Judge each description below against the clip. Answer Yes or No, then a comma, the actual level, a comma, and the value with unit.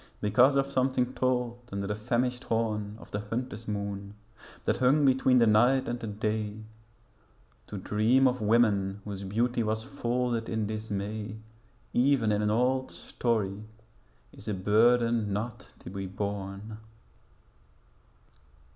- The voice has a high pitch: No, low, 110 Hz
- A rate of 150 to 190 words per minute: No, average, 140 wpm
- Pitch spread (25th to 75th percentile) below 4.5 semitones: Yes, average, 3.1 semitones